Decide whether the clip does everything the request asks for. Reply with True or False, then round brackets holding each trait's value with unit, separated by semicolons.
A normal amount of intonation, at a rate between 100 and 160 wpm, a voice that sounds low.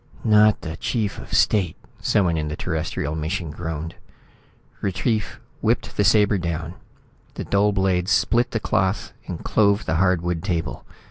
True (3.9 semitones; 145 wpm; 90 Hz)